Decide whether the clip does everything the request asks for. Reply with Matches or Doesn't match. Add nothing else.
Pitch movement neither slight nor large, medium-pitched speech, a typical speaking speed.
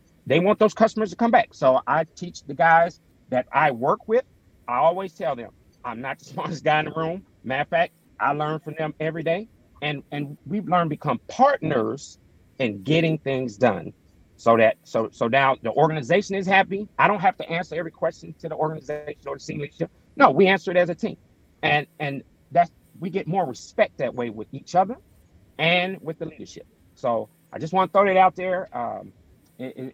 Doesn't match